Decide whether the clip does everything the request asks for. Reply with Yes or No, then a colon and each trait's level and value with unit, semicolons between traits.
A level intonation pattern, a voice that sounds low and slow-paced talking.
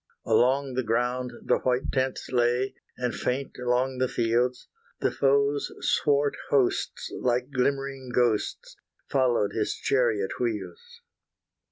Yes: narrow, 2.0 semitones; low, 125 Hz; slow, 120 wpm